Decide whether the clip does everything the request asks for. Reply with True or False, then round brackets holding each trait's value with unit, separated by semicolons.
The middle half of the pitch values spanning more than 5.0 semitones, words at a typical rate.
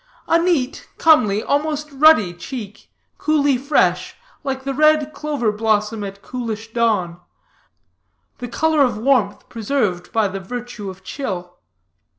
False (5.6 semitones; 130 wpm)